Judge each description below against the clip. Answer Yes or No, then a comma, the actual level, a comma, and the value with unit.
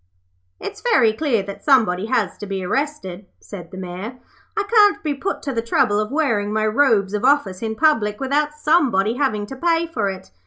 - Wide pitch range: Yes, wide, 6.4 semitones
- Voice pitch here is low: No, high, 225 Hz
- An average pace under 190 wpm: No, average, 195 wpm